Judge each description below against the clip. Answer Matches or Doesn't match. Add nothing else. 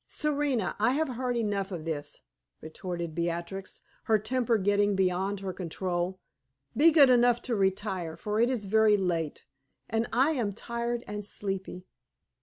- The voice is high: Matches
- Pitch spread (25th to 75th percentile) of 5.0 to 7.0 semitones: Doesn't match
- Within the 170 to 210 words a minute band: Doesn't match